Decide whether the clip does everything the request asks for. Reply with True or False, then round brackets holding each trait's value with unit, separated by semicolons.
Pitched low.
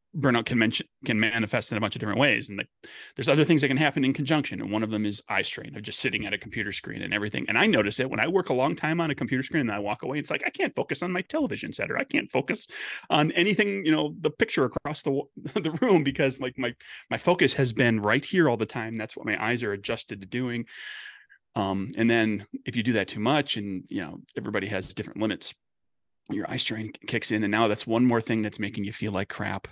True (120 Hz)